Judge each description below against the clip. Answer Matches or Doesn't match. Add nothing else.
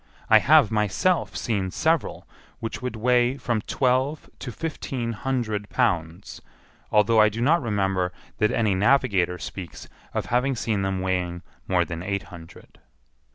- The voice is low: Matches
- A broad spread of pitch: Doesn't match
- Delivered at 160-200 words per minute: Doesn't match